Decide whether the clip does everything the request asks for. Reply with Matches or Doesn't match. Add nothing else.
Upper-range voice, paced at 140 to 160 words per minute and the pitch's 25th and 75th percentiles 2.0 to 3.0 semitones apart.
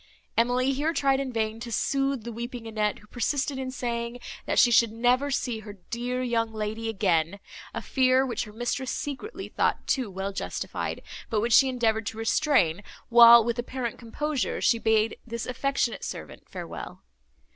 Doesn't match